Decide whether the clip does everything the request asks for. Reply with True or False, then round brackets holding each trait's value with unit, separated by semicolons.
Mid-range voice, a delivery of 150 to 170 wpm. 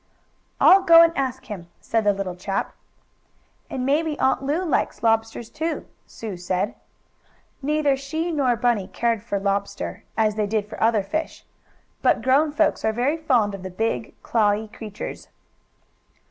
False (230 Hz; 155 wpm)